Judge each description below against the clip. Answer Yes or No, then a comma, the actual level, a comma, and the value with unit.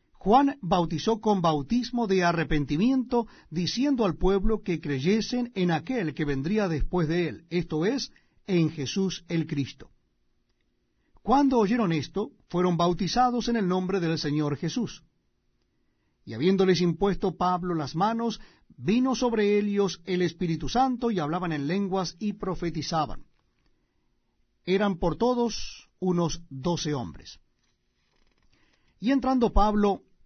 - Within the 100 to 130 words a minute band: Yes, slow, 125 wpm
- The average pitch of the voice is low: No, medium, 185 Hz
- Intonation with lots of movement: No, average, 4.9 semitones